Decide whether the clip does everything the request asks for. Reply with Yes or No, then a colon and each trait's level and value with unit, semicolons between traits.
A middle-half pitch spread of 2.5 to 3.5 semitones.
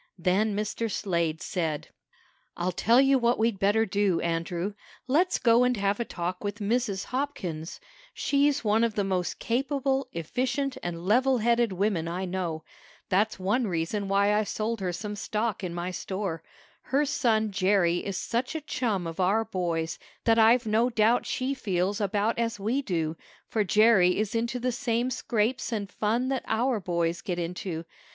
No: average, 4.5 semitones